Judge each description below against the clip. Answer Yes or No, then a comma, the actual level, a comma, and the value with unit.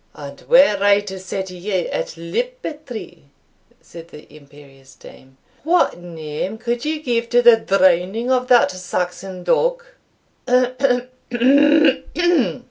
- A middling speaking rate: No, slow, 115 wpm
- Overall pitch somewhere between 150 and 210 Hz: Yes, high, 190 Hz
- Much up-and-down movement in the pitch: Yes, wide, 6.1 semitones